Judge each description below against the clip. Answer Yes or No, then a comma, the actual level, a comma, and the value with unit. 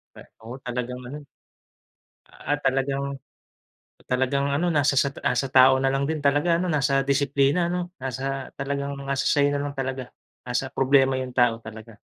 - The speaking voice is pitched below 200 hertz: Yes, low, 135 Hz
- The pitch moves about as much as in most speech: No, narrow, 1.7 semitones